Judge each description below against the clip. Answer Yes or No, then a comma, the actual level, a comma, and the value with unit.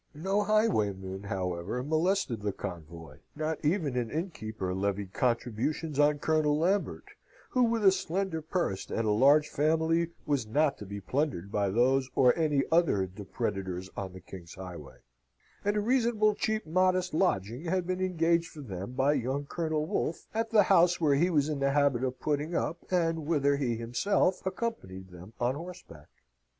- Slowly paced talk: No, average, 165 wpm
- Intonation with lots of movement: Yes, wide, 8.6 semitones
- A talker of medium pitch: Yes, medium, 145 Hz